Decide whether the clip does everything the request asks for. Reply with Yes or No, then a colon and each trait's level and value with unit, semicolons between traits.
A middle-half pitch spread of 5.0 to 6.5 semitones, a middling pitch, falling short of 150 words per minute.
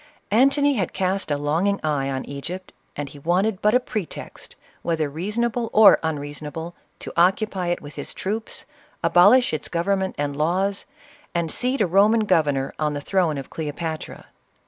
No: average, 5.3 semitones; medium, 175 Hz; average, 170 wpm